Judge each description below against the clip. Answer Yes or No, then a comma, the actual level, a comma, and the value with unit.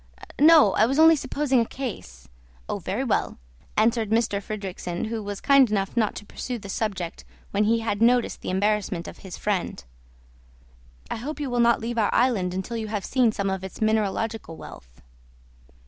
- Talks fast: No, average, 180 wpm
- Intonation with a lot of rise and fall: No, average, 3.4 semitones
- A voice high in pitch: Yes, high, 215 Hz